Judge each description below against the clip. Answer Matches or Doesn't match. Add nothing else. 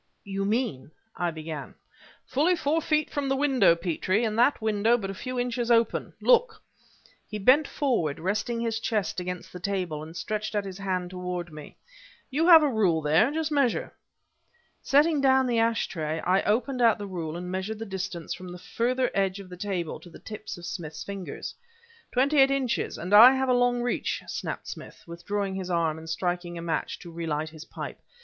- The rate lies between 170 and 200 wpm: Matches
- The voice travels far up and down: Matches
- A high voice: Matches